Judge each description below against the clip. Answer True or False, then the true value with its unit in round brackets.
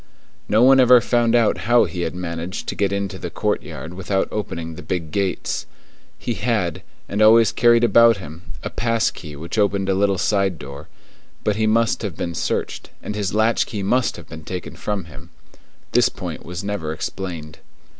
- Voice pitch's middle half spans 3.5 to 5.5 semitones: True (4.5 semitones)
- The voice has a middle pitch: False (100 Hz)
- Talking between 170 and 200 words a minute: True (185 wpm)